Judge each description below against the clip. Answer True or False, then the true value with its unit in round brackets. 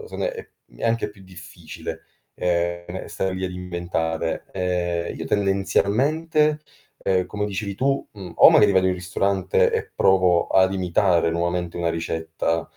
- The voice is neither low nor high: False (90 Hz)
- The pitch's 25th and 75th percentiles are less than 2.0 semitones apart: False (2.3 semitones)